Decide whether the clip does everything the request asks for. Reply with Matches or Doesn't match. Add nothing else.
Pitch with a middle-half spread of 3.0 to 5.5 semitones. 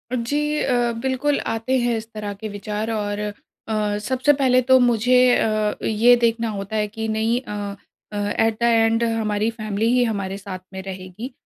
Doesn't match